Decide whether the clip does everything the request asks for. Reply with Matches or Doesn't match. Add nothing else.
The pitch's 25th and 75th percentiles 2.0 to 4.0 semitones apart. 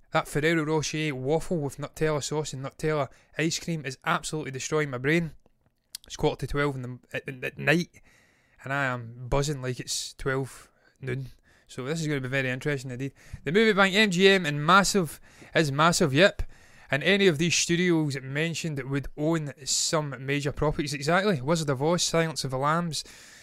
Matches